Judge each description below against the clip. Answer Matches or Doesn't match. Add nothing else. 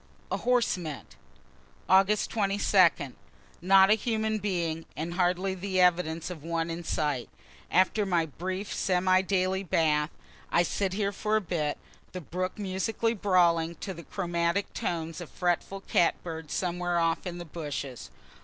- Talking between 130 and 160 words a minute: Matches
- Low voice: Doesn't match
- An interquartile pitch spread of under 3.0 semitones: Matches